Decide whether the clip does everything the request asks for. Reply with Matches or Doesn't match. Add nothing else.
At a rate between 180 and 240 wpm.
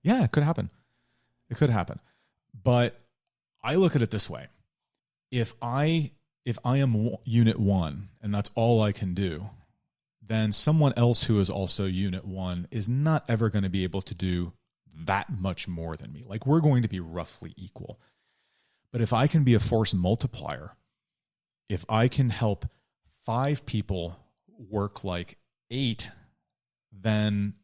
Doesn't match